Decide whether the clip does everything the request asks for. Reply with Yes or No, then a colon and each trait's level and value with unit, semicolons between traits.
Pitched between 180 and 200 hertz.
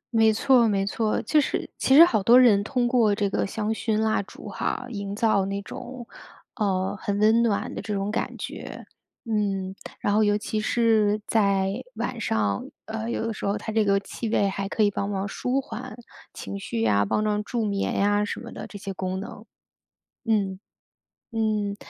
No: high, 210 Hz